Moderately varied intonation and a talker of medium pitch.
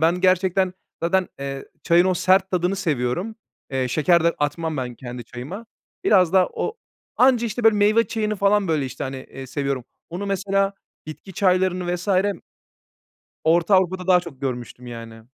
No: wide, 5.9 semitones; medium, 180 Hz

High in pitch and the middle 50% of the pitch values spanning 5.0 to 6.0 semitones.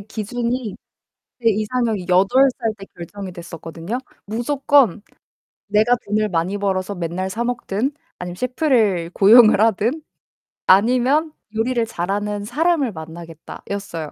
No: high, 210 Hz; average, 4.6 semitones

